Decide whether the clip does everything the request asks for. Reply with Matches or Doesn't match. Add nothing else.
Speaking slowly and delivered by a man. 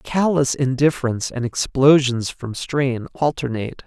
Matches